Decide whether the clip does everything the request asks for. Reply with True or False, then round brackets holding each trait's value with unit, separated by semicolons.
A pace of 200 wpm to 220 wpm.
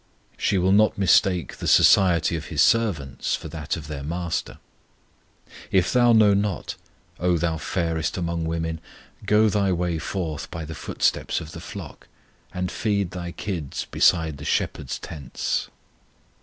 False (150 wpm)